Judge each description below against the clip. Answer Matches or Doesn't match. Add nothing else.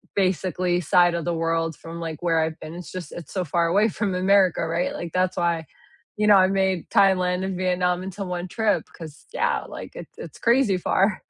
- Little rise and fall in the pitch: Matches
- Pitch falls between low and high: Matches